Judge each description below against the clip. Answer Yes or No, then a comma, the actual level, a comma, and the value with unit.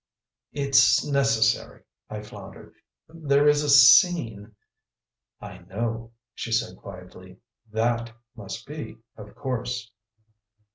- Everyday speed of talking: No, slow, 105 wpm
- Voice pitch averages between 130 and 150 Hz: No, low, 115 Hz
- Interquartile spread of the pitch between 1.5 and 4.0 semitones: No, average, 4.5 semitones